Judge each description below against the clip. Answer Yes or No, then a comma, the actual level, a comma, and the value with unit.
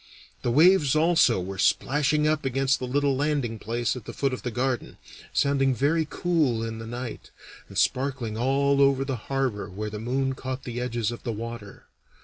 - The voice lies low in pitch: Yes, low, 130 Hz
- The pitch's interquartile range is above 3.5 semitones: No, average, 3.2 semitones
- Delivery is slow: No, average, 185 wpm